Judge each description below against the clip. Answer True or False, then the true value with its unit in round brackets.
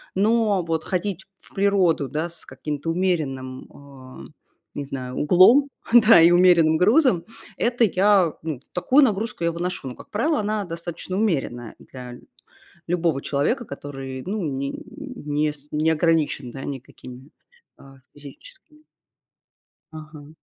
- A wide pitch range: True (5.9 semitones)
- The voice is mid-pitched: True (165 Hz)